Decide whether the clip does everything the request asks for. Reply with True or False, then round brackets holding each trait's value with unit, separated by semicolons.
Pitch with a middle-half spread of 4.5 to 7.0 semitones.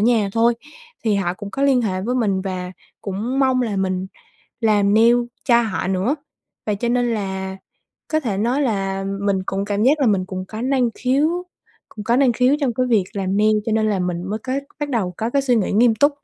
False (4.1 semitones)